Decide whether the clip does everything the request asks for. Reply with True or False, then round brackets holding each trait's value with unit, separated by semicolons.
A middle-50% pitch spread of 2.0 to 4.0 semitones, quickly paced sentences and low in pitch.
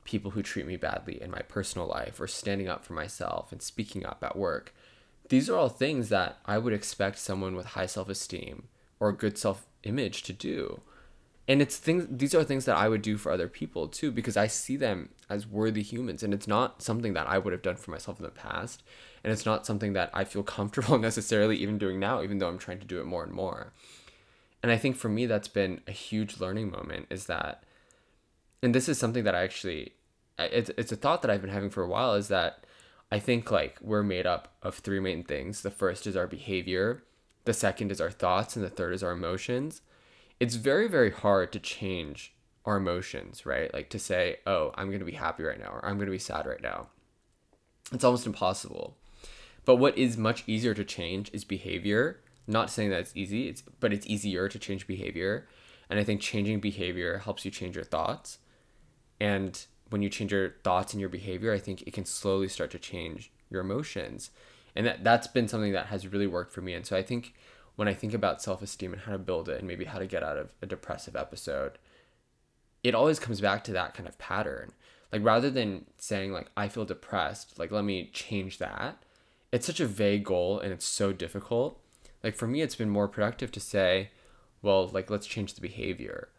True (3.1 semitones; 220 wpm; 105 Hz)